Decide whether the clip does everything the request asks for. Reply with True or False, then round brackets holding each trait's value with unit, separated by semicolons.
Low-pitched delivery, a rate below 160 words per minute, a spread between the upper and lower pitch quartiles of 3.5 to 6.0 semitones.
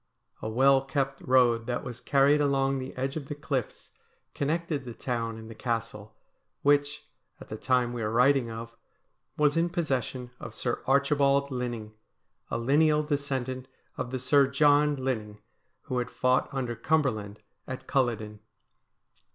False (130 Hz; 150 wpm; 3.0 semitones)